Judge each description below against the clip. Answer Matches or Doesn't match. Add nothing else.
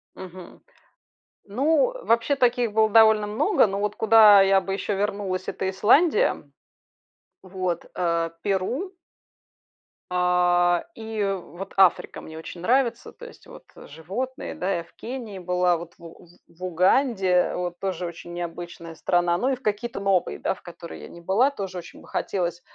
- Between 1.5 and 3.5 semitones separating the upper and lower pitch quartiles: Doesn't match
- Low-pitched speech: Doesn't match